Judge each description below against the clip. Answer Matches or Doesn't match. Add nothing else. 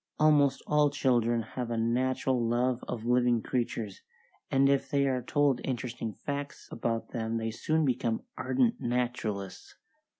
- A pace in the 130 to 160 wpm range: Matches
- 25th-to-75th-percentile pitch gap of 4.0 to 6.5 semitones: Doesn't match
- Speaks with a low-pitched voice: Matches